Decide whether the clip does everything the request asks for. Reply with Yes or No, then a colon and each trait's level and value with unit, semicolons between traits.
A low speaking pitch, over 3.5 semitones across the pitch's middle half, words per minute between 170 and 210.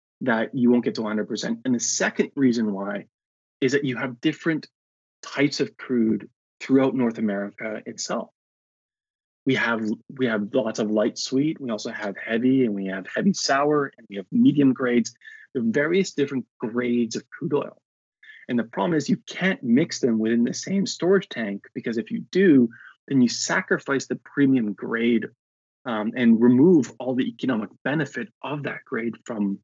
Yes: low, 125 Hz; average, 4.3 semitones; average, 175 wpm